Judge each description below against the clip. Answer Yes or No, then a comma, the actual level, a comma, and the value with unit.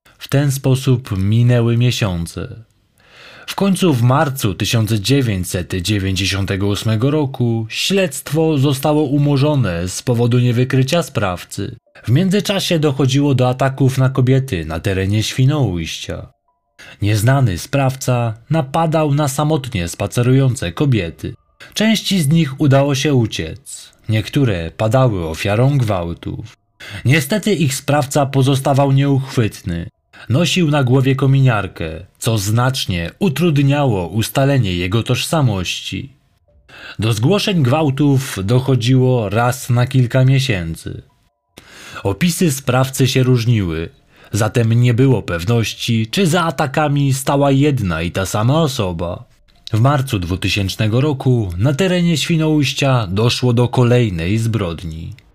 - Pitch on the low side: Yes, low, 125 Hz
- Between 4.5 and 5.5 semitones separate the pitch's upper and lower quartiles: Yes, average, 5.1 semitones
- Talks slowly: Yes, slow, 105 wpm